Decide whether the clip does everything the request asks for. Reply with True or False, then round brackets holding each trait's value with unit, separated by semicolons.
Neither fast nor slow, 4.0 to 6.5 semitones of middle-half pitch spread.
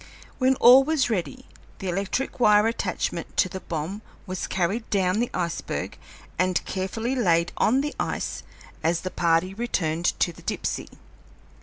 True (150 wpm; 5.4 semitones)